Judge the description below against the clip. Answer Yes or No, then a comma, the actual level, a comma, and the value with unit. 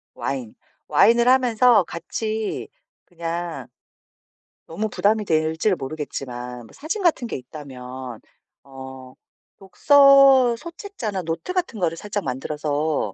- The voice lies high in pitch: No, medium, 170 Hz